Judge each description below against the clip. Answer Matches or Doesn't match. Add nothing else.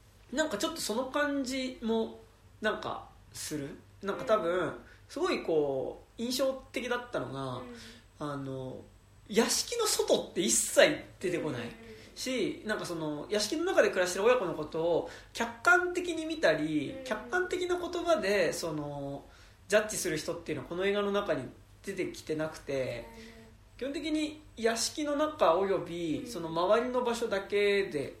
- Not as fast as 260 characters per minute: Doesn't match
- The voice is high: Matches